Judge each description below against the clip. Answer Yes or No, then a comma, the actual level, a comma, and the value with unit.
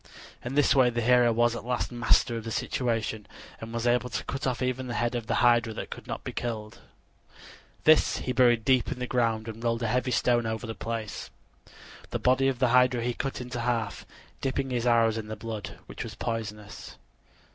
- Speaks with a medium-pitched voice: No, low, 120 Hz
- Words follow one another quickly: Yes, fast, 210 wpm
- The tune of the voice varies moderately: No, narrow, 1.8 semitones